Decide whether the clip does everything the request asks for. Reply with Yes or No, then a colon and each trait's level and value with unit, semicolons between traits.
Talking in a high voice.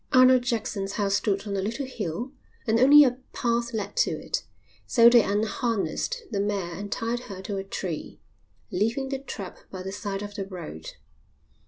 Yes: high, 210 Hz